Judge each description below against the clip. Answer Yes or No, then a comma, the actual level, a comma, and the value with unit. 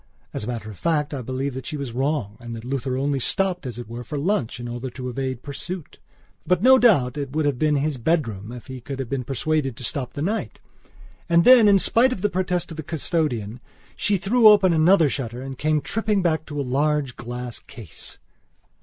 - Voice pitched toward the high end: No, medium, 140 Hz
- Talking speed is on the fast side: Yes, fast, 220 wpm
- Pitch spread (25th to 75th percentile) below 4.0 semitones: No, average, 5.3 semitones